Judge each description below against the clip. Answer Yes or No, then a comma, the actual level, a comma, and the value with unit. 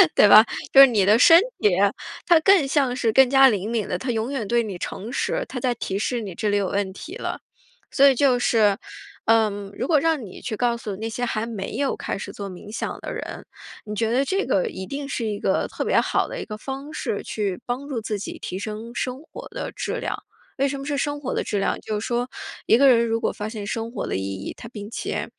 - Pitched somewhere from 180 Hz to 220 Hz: No, high, 230 Hz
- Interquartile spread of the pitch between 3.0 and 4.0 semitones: No, average, 4.4 semitones